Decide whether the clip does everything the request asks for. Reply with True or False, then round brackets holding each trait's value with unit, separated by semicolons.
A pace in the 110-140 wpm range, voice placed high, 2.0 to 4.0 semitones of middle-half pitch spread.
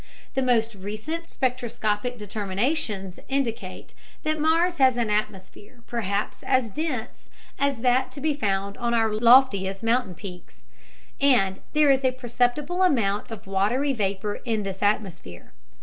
False (135 wpm; 235 Hz; 4.8 semitones)